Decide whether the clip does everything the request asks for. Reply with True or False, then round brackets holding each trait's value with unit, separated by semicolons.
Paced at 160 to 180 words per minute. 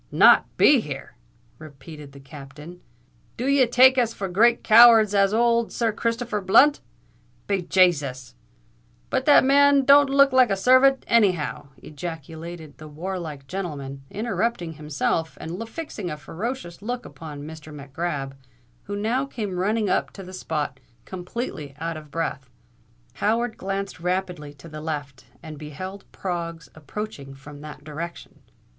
False (145 wpm)